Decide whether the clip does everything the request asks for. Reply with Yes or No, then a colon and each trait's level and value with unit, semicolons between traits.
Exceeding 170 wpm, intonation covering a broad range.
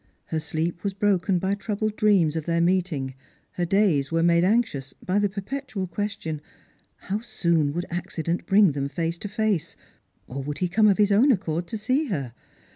No: average, 190 wpm; average, 4.1 semitones